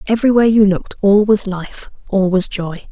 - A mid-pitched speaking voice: No, high, 200 Hz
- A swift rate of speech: No, average, 185 wpm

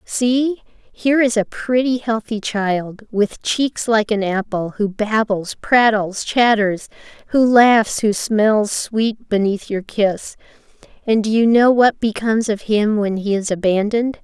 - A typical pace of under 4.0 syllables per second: Yes, 3.8 syllables/s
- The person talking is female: Yes, female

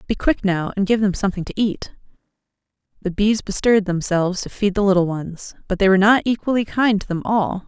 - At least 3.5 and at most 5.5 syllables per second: No, 6.1 syllables/s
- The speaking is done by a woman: Yes, female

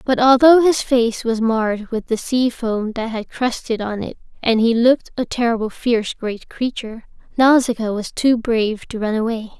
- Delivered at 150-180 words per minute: No, average, 190 wpm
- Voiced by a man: No, female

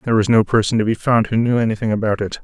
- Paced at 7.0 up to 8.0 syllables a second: Yes, 7.4 syllables/s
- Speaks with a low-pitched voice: Yes, low, 110 Hz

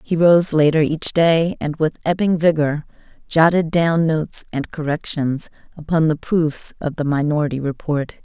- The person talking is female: Yes, female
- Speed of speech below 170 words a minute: Yes, average, 155 wpm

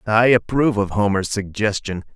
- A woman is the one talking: No, male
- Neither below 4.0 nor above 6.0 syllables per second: Yes, 5.2 syllables/s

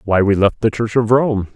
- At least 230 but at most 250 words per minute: No, fast, 270 wpm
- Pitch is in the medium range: No, low, 110 Hz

